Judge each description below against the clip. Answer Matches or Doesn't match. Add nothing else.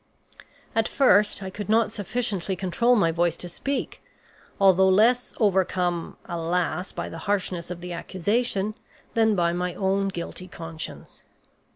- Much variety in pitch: Doesn't match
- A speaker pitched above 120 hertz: Matches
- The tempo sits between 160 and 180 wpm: Doesn't match